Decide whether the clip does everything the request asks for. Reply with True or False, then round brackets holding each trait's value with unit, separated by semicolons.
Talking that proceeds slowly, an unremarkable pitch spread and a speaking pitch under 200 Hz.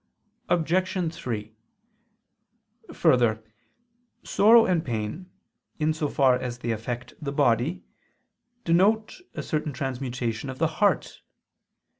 False (105 wpm; 6.0 semitones; 140 Hz)